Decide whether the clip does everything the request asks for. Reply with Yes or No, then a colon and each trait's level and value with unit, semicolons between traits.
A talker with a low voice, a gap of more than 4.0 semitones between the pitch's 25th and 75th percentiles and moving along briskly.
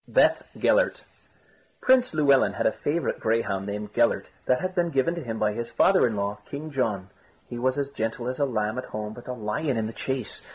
Yes: low, 125 Hz; average, 5.0 semitones; fast, 215 wpm